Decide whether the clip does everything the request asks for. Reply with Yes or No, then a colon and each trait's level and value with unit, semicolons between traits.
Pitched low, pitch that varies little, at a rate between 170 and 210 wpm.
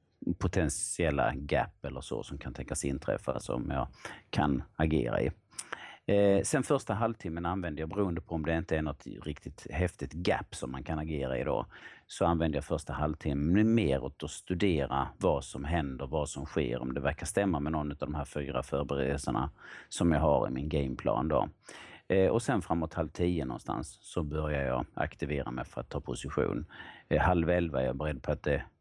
No: very low, 75 Hz; average, 3.9 semitones; fast, 195 wpm